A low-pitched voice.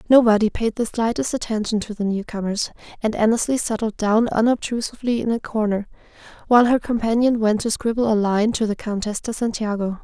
No: high, 220 Hz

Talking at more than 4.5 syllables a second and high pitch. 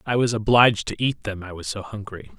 No: 5.9 syllables/s; low, 105 Hz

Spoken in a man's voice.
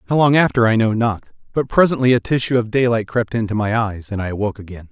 Yes: male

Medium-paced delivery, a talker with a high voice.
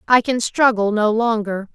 Yes: average, 170 wpm; high, 225 Hz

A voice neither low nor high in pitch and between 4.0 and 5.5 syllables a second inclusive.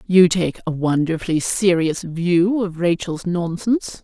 Yes: medium, 175 Hz; 4.2 syllables/s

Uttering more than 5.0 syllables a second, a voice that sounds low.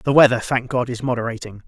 Yes: 6.2 syllables/s; low, 120 Hz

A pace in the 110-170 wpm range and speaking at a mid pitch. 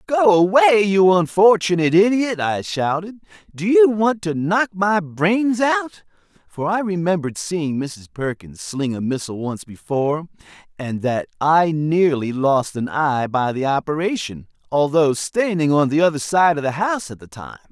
Yes: average, 165 wpm; medium, 170 Hz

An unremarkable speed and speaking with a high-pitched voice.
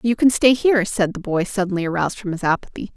No: fast, 245 wpm; high, 205 Hz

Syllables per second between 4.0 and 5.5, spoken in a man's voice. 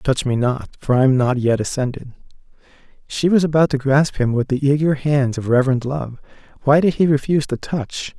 Yes: 5.4 syllables/s; male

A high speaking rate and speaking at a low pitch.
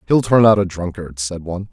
Yes: fast, 245 wpm; very low, 95 Hz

